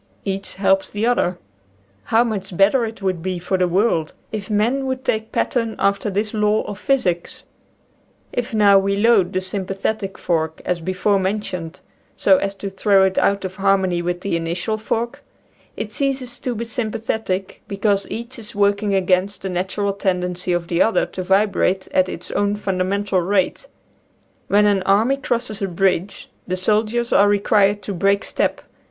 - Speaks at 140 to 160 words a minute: No, average, 170 wpm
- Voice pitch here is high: Yes, high, 200 Hz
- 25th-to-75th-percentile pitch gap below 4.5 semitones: Yes, narrow, 2.5 semitones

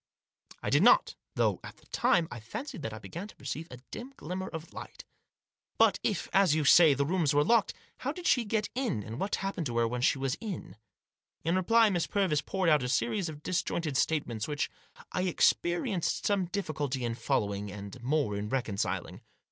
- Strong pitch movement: Yes, wide, 7.2 semitones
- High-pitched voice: No, medium, 155 Hz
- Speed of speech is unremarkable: No, fast, 210 wpm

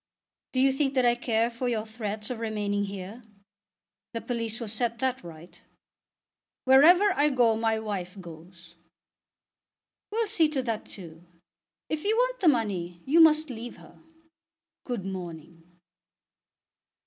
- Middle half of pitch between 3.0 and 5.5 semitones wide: Yes, average, 5.1 semitones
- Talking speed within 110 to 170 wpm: Yes, average, 140 wpm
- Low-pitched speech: No, high, 230 Hz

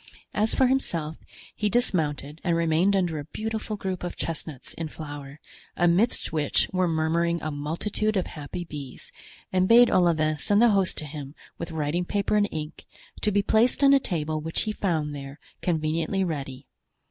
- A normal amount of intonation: Yes, average, 4.7 semitones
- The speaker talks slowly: No, average, 170 wpm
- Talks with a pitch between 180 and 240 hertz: No, medium, 170 Hz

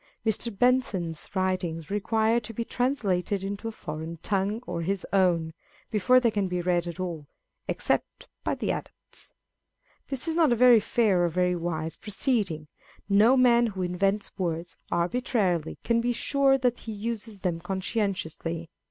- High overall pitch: Yes, high, 200 Hz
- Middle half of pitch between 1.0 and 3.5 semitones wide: No, average, 4.9 semitones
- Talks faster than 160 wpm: No, average, 155 wpm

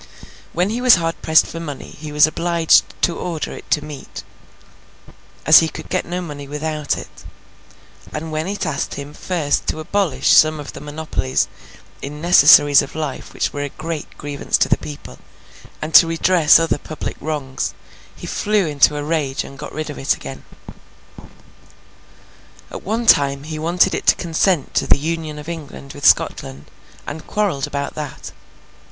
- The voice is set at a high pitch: No, medium, 155 Hz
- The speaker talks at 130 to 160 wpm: No, average, 170 wpm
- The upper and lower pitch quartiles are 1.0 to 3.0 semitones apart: Yes, narrow, 2.5 semitones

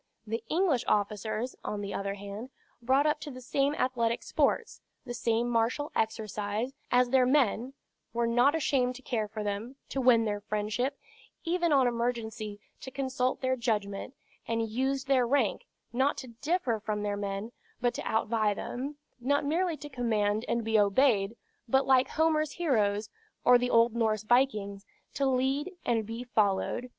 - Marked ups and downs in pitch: No, average, 3.7 semitones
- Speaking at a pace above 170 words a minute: No, average, 165 wpm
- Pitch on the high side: Yes, high, 240 Hz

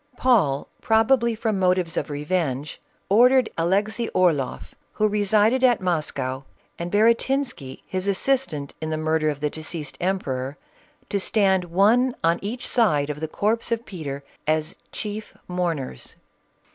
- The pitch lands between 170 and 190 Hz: Yes, medium, 185 Hz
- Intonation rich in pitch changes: Yes, wide, 6.2 semitones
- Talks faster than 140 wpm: No, slow, 135 wpm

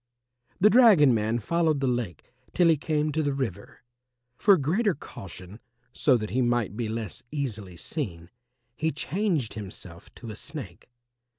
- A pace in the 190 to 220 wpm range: No, average, 155 wpm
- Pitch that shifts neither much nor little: No, wide, 6.7 semitones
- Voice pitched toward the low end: Yes, low, 130 Hz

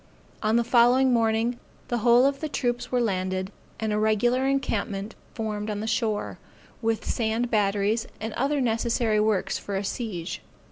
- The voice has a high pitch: Yes, high, 225 Hz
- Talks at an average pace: Yes, average, 160 wpm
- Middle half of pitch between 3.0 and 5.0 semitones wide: No, narrow, 2.4 semitones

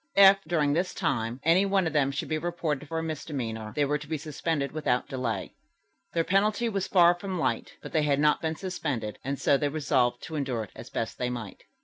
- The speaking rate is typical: No, fast, 225 wpm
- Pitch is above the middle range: No, medium, 150 Hz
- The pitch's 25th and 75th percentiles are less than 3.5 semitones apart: No, average, 4.3 semitones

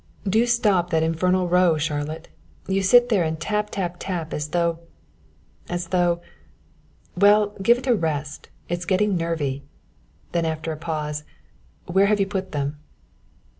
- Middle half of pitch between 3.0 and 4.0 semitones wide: Yes, average, 3.5 semitones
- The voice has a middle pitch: Yes, medium, 175 Hz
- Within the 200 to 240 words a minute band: No, average, 150 wpm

